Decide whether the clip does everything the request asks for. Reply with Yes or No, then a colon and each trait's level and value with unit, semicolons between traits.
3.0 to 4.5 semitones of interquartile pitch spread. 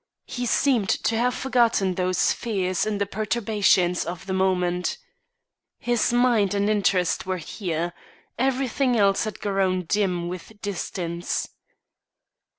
Yes: average, 3.8 semitones